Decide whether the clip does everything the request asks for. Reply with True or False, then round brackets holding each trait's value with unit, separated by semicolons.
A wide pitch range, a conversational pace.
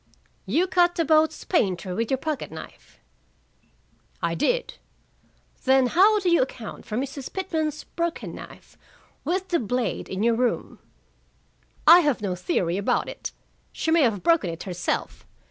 True (7.9 semitones; 150 wpm)